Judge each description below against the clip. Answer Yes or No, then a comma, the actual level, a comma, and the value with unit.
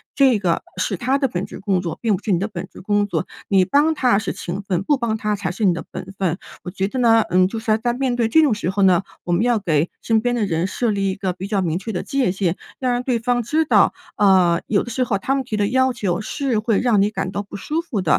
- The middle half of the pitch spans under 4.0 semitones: No, average, 4.5 semitones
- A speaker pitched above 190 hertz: Yes, high, 210 Hz